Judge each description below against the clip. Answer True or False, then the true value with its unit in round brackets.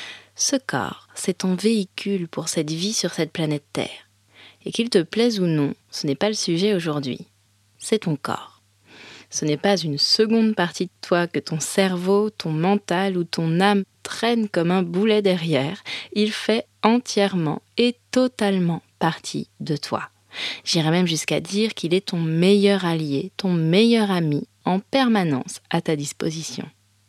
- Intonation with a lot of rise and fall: False (4.7 semitones)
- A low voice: False (180 Hz)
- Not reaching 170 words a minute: True (160 wpm)